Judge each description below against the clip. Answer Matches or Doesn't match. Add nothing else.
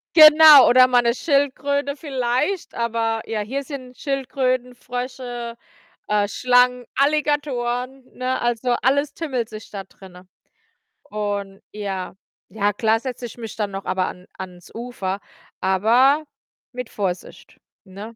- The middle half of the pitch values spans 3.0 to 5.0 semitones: Matches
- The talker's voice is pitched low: Doesn't match